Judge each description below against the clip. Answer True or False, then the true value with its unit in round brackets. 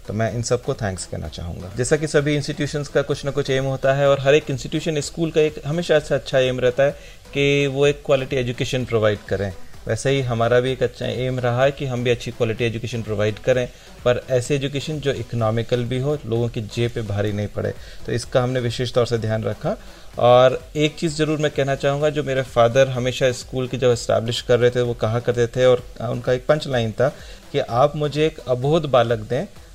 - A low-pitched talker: True (125 Hz)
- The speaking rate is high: True (225 wpm)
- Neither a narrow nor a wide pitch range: True (3.1 semitones)